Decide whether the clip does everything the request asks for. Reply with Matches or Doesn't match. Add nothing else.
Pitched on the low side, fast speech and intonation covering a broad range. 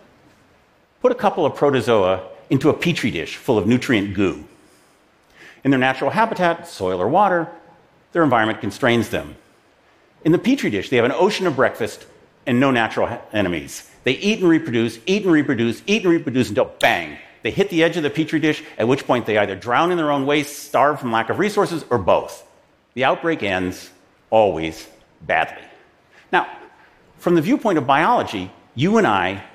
Doesn't match